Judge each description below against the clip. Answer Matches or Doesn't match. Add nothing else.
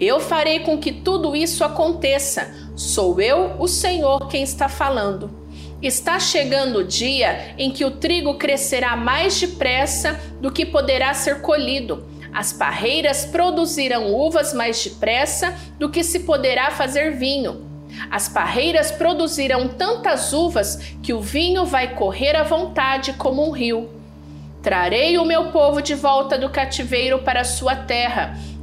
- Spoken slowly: Doesn't match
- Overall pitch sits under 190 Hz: Doesn't match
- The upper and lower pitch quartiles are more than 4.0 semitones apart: Doesn't match